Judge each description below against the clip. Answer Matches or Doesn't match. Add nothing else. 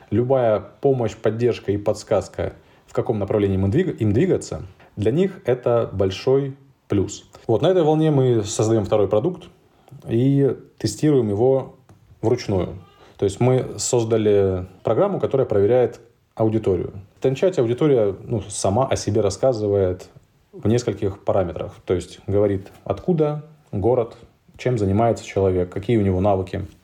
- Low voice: Matches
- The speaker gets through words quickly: Doesn't match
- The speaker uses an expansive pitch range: Doesn't match